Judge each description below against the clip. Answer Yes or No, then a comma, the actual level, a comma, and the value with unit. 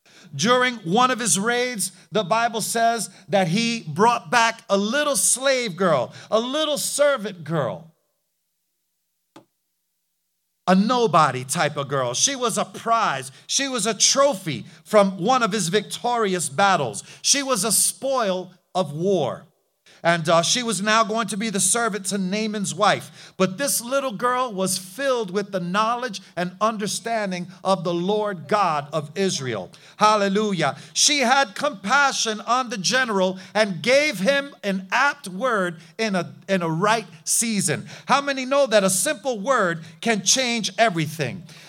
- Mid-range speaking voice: No, high, 210 Hz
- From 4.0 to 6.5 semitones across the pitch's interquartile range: Yes, average, 4.7 semitones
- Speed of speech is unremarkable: Yes, average, 150 wpm